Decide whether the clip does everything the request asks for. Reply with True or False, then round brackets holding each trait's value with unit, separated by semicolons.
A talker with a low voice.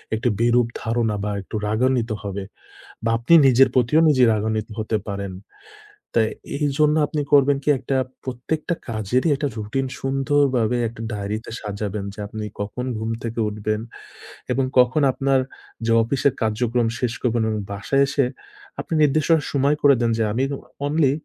True (120 Hz)